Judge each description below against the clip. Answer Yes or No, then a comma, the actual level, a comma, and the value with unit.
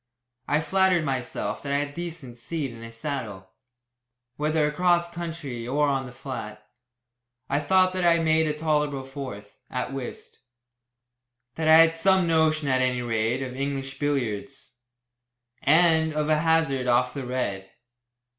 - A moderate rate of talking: Yes, average, 155 wpm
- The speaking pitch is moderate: Yes, medium, 145 Hz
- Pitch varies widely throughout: No, average, 4.1 semitones